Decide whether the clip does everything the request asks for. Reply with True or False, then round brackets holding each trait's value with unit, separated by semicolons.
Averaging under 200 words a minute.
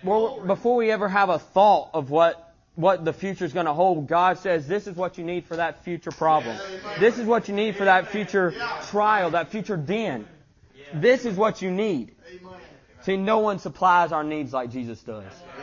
False (205 wpm)